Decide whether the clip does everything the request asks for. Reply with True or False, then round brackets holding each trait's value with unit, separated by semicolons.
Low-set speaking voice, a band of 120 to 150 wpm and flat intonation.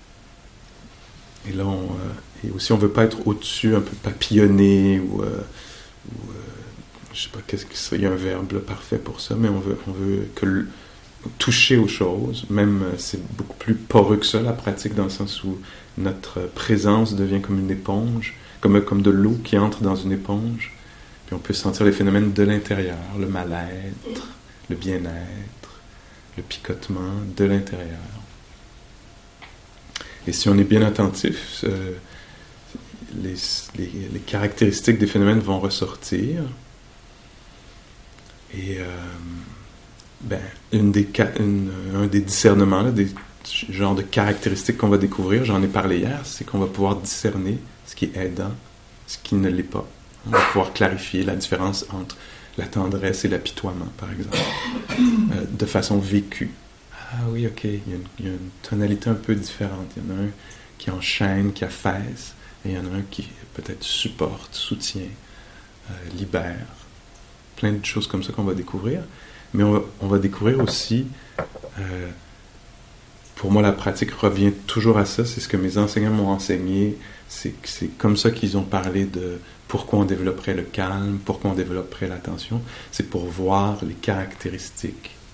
False (100 Hz; 170 wpm; 2.0 semitones)